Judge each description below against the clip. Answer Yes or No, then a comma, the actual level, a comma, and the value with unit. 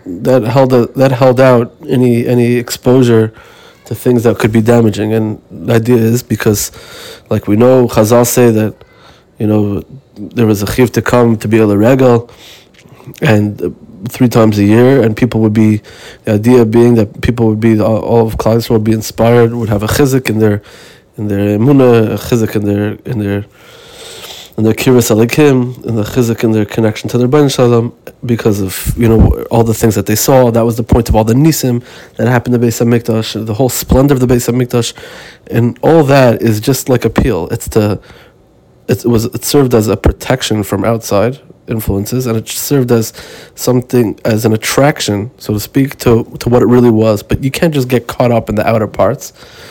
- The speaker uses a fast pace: Yes, fast, 200 wpm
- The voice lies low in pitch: Yes, low, 115 Hz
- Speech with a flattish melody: Yes, narrow, 2.3 semitones